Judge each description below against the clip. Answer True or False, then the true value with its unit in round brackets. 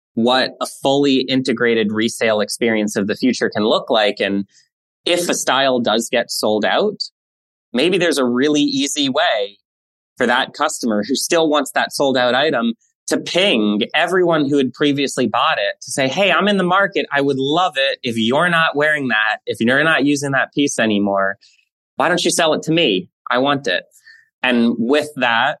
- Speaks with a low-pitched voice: True (130 Hz)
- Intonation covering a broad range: True (5.9 semitones)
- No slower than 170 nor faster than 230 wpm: True (190 wpm)